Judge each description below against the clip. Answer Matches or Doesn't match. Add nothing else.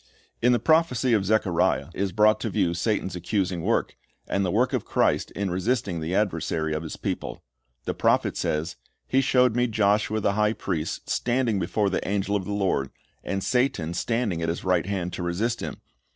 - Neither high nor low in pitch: Doesn't match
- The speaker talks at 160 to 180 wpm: Doesn't match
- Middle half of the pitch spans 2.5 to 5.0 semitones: Matches